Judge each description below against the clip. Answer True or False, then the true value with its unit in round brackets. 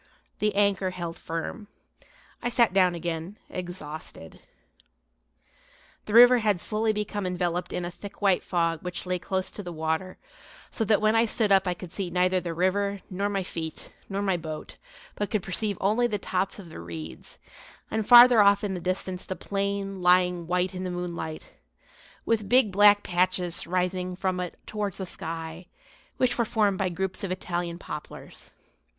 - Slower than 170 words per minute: False (175 wpm)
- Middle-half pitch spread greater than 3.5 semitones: False (2.6 semitones)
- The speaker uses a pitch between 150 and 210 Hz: True (185 Hz)